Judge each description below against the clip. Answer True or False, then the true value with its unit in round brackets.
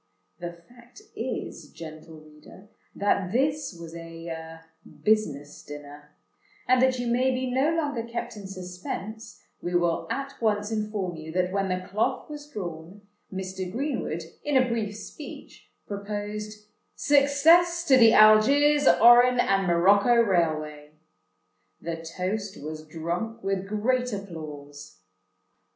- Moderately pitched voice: False (205 Hz)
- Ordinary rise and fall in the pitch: False (6.3 semitones)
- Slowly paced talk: True (130 wpm)